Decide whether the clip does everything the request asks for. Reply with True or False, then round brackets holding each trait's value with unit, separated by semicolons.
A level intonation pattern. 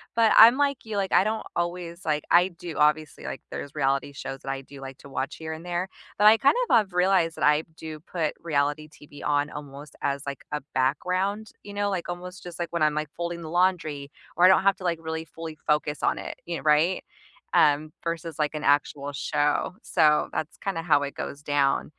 False (3.5 semitones)